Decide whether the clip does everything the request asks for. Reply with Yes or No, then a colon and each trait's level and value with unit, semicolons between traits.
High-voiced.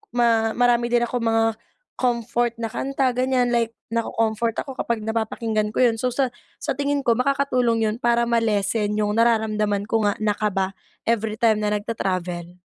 Yes: high, 230 Hz